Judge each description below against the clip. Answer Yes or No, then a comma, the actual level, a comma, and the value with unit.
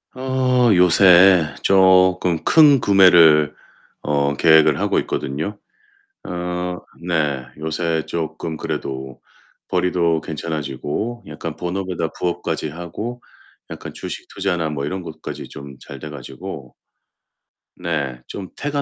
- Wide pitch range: No, average, 3.8 semitones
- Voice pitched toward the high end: No, very low, 85 Hz